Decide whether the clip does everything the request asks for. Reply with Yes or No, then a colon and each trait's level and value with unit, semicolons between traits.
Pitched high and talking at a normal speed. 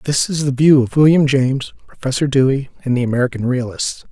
No: low, 135 Hz; average, 190 wpm